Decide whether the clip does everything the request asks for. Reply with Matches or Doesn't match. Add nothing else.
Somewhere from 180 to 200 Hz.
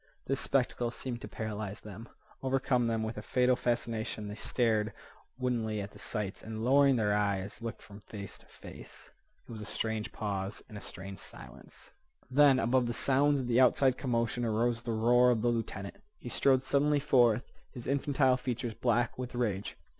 Doesn't match